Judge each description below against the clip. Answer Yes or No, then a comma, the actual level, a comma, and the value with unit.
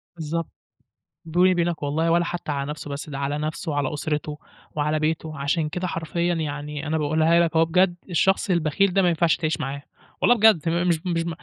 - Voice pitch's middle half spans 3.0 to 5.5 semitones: No, narrow, 2.5 semitones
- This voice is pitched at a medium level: Yes, medium, 160 Hz